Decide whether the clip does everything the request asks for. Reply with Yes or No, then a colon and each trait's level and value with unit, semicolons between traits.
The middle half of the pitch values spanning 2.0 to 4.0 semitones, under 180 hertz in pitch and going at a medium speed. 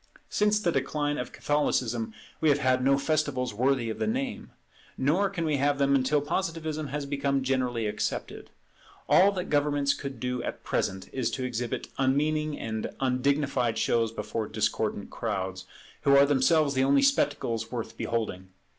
Yes: average, 3.5 semitones; medium, 140 Hz; average, 160 wpm